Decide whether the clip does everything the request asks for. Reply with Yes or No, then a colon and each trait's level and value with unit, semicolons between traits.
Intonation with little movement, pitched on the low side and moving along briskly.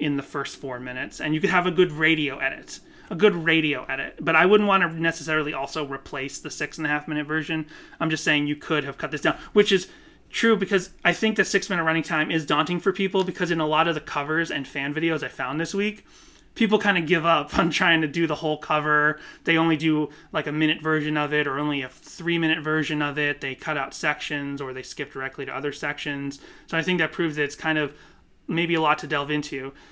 No: narrow, 2.3 semitones; medium, 155 Hz; fast, 250 wpm